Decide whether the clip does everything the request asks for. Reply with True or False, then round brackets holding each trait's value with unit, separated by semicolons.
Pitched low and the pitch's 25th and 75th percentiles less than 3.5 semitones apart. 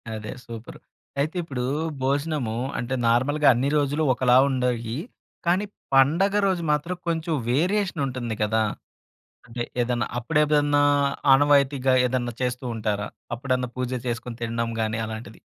False (130 Hz; 3.8 semitones)